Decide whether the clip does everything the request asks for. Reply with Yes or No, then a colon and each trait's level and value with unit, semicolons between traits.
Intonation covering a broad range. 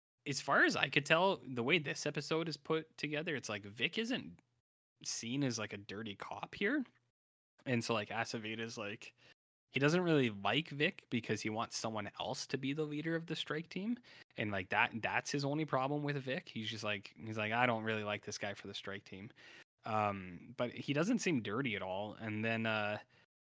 Yes: wide, 5.7 semitones